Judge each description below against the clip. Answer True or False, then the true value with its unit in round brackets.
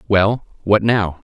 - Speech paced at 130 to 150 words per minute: True (135 wpm)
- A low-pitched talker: True (100 Hz)